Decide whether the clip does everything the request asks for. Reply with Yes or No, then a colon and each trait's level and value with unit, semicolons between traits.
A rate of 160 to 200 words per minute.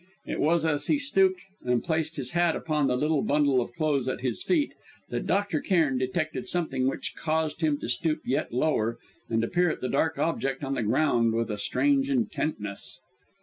Yes: average, 195 wpm